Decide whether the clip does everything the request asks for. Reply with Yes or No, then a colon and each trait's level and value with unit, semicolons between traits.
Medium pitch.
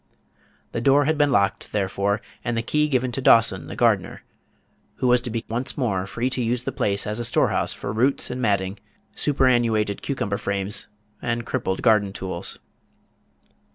No: low, 115 Hz